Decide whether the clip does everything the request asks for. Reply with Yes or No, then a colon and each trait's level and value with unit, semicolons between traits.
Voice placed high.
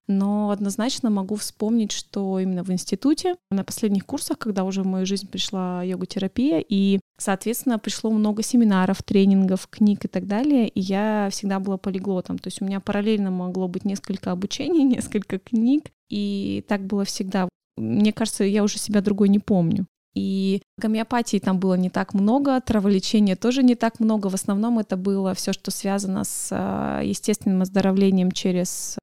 Yes: high, 200 Hz